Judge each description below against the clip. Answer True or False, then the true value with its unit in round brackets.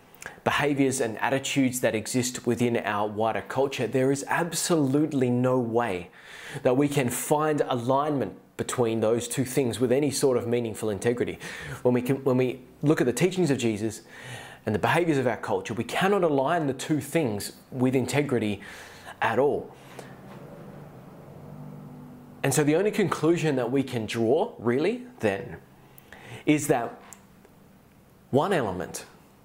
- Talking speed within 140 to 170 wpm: True (145 wpm)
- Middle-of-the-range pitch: False (130 Hz)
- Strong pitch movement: False (4.0 semitones)